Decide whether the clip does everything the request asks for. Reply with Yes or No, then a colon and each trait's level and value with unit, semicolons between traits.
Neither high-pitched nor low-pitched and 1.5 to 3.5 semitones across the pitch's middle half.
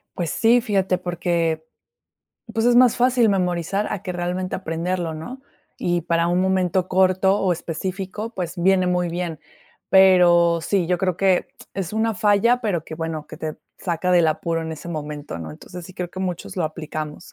Yes: medium, 180 Hz; narrow, 2.4 semitones